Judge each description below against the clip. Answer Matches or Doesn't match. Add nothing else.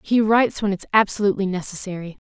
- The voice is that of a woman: Matches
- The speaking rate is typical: Matches